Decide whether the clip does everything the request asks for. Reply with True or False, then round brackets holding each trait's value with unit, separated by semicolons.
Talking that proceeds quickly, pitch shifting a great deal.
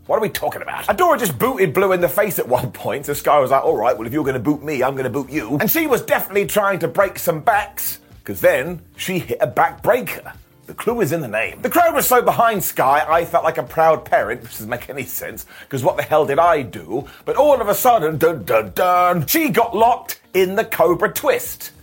True (245 wpm; 6.5 semitones)